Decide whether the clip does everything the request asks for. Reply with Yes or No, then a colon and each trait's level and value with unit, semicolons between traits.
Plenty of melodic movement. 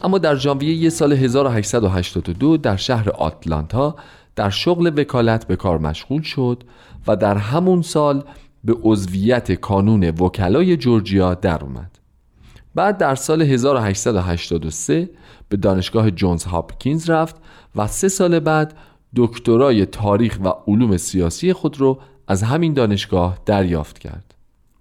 Yes: wide, 7.2 semitones